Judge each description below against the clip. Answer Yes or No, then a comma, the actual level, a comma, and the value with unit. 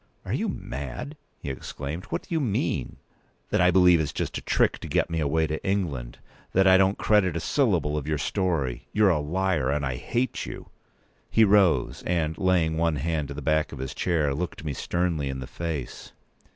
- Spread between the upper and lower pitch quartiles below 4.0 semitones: No, average, 4.4 semitones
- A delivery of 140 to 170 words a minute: No, fast, 205 wpm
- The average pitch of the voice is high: No, very low, 80 Hz